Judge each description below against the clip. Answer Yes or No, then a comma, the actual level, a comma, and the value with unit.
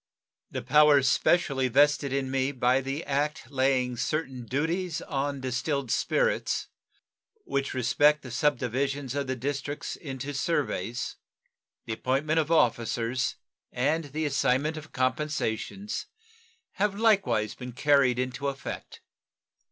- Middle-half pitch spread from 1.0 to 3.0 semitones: Yes, average, 2.7 semitones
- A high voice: No, medium, 140 Hz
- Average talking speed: No, slow, 120 wpm